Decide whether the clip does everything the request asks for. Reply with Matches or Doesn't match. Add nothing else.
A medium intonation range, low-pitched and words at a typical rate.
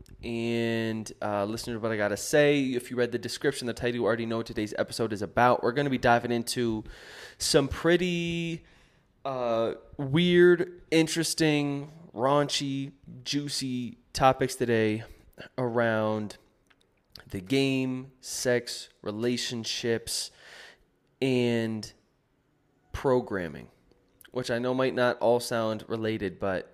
Doesn't match